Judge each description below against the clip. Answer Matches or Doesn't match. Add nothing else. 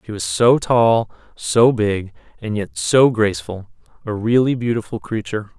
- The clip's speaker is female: Doesn't match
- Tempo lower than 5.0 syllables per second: Matches